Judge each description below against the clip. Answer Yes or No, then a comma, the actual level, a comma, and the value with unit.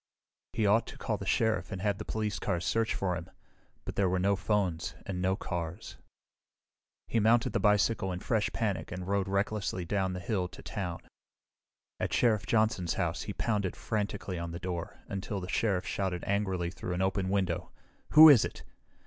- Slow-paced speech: No, average, 185 wpm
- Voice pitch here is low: Yes, very low, 95 Hz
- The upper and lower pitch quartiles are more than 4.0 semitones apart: No, narrow, 2.6 semitones